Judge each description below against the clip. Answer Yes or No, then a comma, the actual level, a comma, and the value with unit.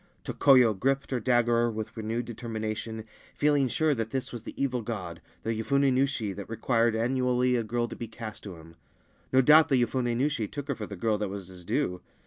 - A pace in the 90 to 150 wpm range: No, fast, 205 wpm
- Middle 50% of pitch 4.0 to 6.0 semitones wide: No, average, 3.1 semitones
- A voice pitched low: Yes, low, 115 Hz